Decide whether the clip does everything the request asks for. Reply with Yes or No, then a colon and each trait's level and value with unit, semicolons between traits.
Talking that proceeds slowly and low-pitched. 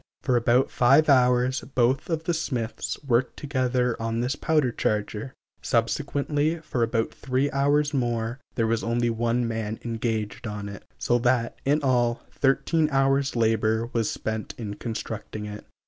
No: average, 150 wpm; low, 120 Hz